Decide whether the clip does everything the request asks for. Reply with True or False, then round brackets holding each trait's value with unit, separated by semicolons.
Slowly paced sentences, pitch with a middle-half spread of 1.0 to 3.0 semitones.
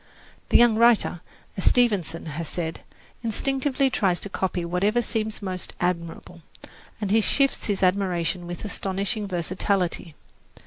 False (130 wpm; 3.9 semitones)